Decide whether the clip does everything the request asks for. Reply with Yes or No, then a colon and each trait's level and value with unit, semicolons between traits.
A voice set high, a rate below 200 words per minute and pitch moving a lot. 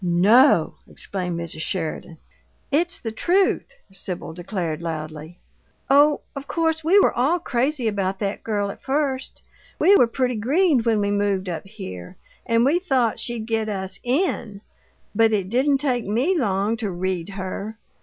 Yes: high, 220 Hz; average, 155 wpm; wide, 6.2 semitones